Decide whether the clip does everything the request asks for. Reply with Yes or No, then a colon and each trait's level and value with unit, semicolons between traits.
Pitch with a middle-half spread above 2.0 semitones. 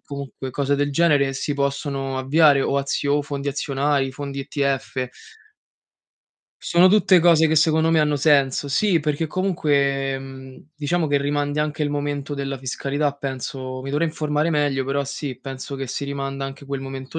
No: narrow, 1.6 semitones